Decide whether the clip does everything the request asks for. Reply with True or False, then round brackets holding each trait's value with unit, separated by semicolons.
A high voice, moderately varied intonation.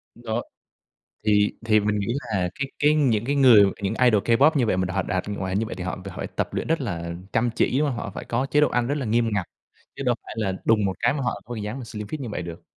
False (115 Hz; 4.2 semitones)